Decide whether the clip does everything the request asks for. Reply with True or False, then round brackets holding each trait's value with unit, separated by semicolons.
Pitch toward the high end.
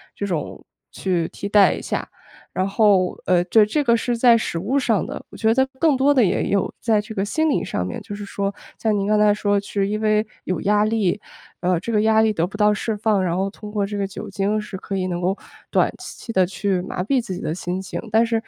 True (205 Hz)